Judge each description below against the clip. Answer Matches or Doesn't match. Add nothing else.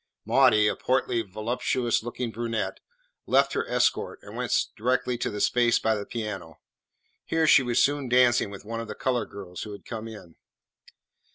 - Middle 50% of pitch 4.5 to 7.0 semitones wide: Doesn't match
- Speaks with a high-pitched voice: Doesn't match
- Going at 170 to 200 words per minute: Matches